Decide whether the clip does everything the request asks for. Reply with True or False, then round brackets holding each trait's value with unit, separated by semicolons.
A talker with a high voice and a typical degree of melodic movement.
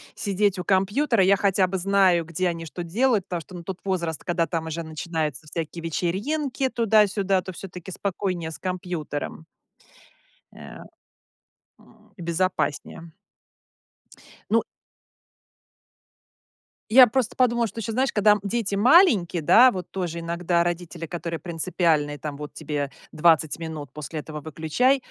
False (180 Hz; 3.7 semitones)